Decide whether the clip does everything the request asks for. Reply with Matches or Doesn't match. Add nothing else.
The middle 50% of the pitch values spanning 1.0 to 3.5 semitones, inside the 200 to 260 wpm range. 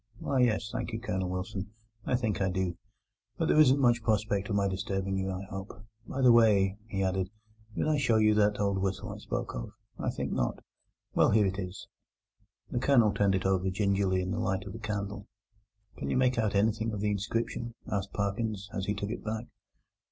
Matches